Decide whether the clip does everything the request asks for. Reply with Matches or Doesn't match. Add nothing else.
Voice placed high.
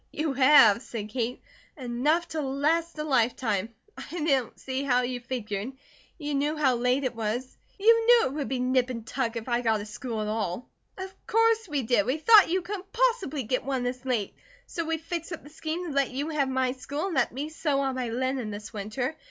Matches